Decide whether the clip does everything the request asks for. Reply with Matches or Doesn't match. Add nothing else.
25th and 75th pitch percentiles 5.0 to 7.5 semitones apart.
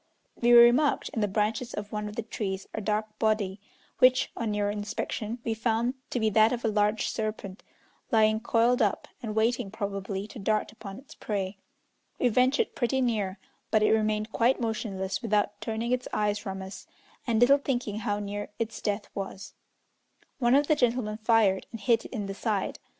Doesn't match